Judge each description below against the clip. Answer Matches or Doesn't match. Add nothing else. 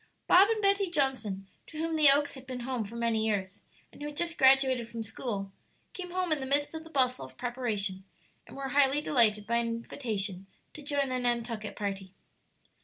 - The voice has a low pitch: Doesn't match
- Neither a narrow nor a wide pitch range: Matches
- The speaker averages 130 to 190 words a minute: Doesn't match